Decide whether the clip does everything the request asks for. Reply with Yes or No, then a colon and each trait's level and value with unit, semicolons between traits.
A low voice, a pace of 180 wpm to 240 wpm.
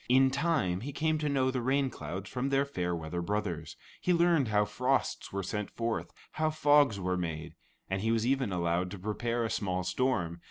Yes: low, 115 Hz; average, 200 wpm